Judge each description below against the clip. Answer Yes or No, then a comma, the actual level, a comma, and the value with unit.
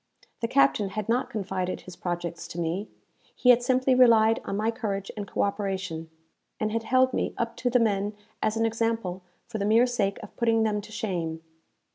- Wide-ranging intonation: No, average, 3.0 semitones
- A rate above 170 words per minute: Yes, average, 195 wpm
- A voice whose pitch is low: No, high, 215 Hz